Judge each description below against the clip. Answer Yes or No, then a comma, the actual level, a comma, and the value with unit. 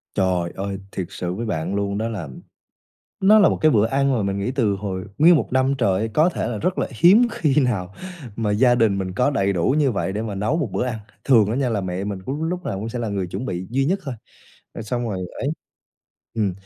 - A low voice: Yes, low, 110 Hz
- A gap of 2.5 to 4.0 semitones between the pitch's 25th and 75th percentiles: No, average, 5.2 semitones